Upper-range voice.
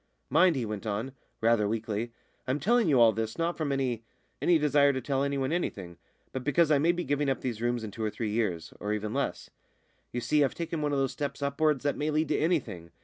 No: low, 135 Hz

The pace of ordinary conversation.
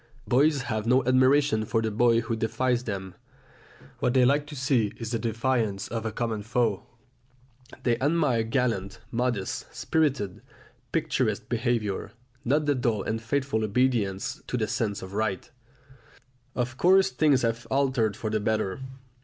Yes: average, 150 wpm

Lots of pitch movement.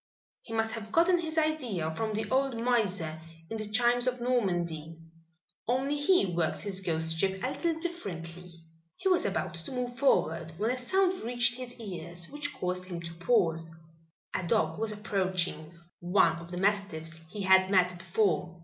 Yes: wide, 6.2 semitones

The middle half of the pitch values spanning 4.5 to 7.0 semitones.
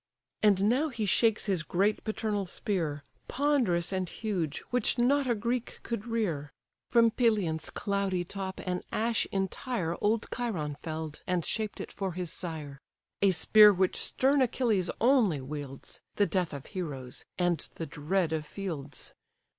Yes: average, 5.3 semitones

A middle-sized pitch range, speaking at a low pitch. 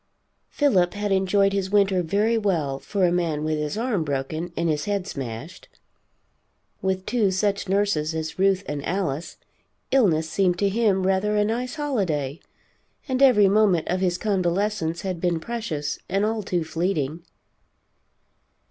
No: average, 4.2 semitones; high, 190 Hz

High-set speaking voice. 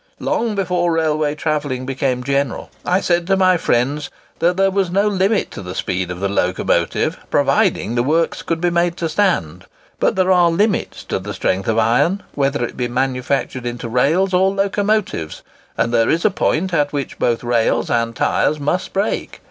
No: medium, 155 Hz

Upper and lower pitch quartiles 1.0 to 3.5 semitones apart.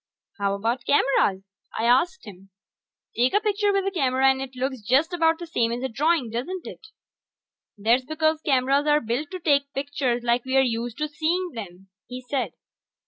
No: average, 4.7 semitones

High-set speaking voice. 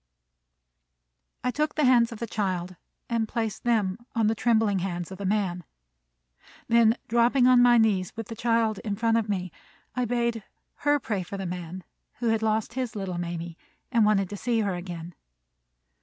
Yes: high, 220 Hz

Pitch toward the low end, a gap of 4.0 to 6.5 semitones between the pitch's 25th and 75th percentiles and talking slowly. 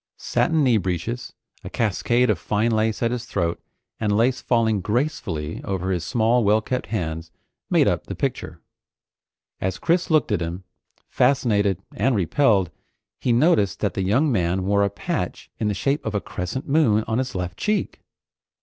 No: low, 110 Hz; average, 4.7 semitones; average, 170 wpm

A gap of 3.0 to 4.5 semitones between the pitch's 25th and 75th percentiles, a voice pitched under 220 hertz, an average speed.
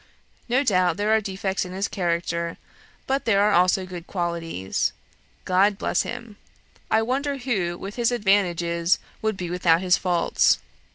Yes: average, 3.6 semitones; high, 190 Hz; average, 155 wpm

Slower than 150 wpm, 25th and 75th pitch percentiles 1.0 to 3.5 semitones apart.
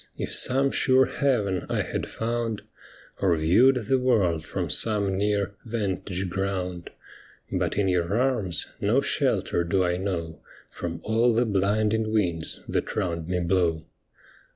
No: average, 140 wpm; average, 4.2 semitones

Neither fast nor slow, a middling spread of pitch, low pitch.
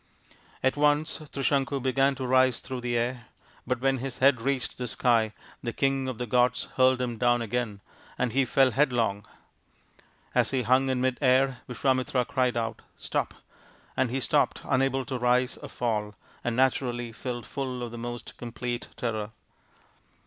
No: average, 170 wpm; narrow, 1.7 semitones; low, 125 Hz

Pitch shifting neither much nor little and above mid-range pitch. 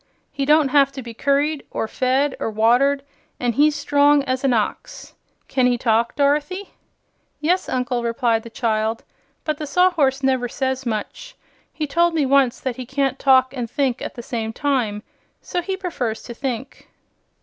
Yes: average, 3.3 semitones; very high, 265 Hz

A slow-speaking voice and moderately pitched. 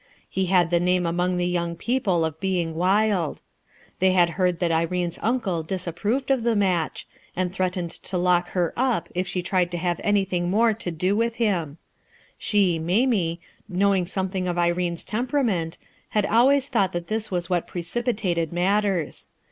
No: average, 170 wpm; medium, 180 Hz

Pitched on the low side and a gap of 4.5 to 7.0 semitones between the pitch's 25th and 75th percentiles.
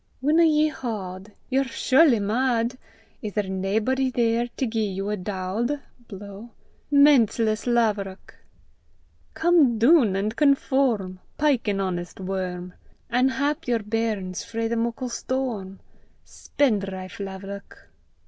No: high, 225 Hz; average, 5.1 semitones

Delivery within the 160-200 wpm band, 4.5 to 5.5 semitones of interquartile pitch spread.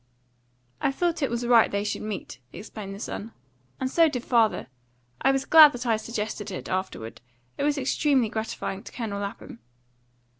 Yes: average, 175 wpm; average, 4.8 semitones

